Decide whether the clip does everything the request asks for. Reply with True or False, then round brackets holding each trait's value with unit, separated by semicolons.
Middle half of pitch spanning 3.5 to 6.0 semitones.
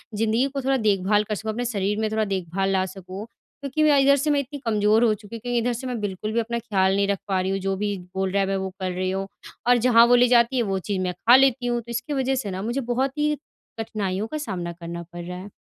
True (4.1 semitones)